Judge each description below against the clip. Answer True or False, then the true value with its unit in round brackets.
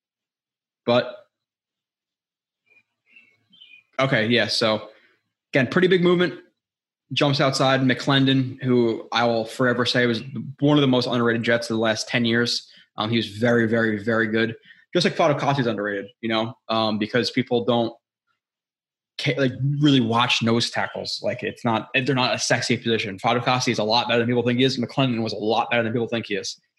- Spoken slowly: False (175 wpm)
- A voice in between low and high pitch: False (120 Hz)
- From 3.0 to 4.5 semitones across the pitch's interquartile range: False (2.5 semitones)